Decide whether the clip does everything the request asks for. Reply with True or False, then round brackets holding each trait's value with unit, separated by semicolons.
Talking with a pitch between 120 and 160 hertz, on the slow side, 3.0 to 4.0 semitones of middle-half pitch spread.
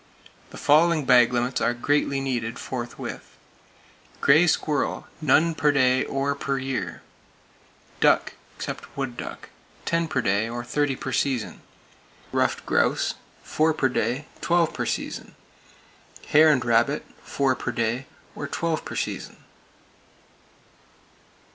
True (135 Hz; 125 wpm; 3.6 semitones)